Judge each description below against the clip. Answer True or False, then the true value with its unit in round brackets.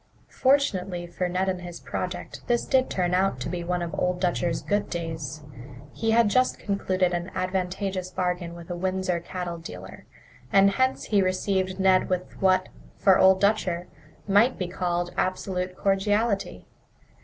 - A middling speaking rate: True (155 wpm)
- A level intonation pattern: True (1.8 semitones)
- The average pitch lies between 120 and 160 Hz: False (185 Hz)